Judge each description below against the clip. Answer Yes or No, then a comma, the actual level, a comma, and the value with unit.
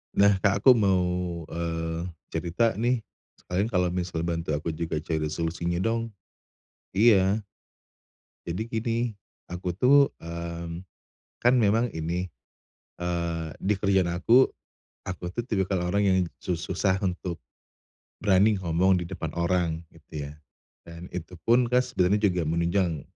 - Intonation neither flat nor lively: Yes, average, 3.3 semitones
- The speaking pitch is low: Yes, very low, 90 Hz